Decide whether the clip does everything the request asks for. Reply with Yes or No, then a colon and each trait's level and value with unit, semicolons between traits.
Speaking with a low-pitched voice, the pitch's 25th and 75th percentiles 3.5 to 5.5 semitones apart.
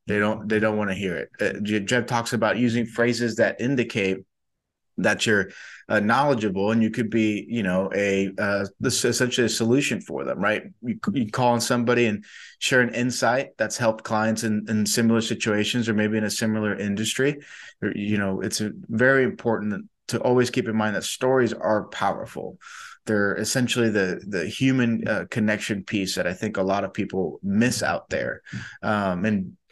No: low, 110 Hz; average, 2.7 semitones